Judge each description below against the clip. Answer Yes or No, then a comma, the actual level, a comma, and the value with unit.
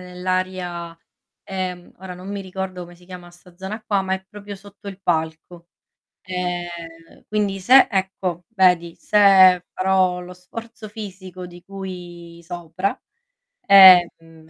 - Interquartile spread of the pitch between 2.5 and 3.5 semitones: No, narrow, 1.7 semitones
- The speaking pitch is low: No, medium, 185 Hz